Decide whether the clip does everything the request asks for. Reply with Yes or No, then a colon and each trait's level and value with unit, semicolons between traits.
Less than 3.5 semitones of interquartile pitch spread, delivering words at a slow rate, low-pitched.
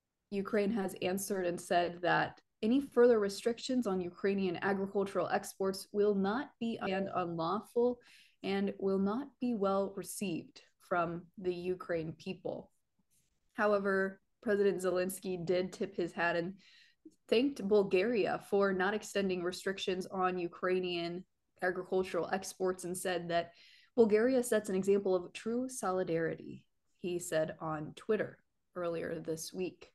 No: narrow, 2.4 semitones; slow, 125 wpm; high, 190 Hz